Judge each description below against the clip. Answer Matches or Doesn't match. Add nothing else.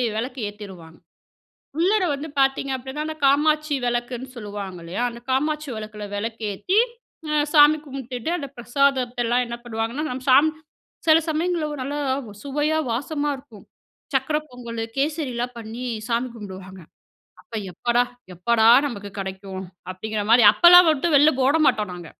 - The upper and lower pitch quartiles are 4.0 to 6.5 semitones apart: Matches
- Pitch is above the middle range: Matches